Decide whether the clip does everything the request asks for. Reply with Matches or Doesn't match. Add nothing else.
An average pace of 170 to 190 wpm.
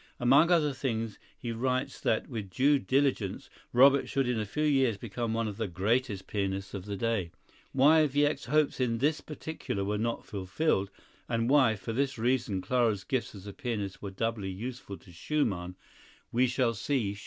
Matches